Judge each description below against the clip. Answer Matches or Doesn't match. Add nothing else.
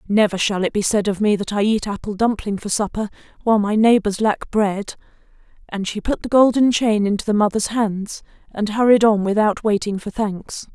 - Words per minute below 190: Doesn't match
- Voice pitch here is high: Matches